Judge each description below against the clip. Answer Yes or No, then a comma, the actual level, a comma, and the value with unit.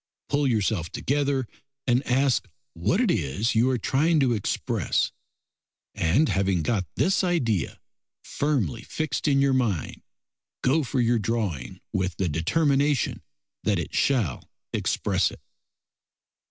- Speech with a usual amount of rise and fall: No, wide, 6.4 semitones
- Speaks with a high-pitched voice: No, low, 125 Hz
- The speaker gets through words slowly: Yes, slow, 125 wpm